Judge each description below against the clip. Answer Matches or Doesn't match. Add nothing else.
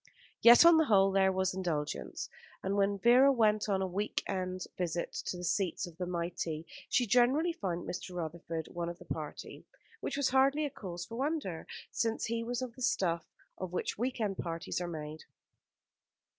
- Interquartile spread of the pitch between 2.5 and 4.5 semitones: Doesn't match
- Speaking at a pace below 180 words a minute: Doesn't match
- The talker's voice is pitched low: Doesn't match